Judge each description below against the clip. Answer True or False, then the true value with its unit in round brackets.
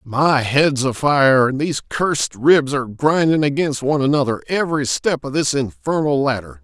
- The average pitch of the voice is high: False (135 Hz)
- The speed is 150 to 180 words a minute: True (170 wpm)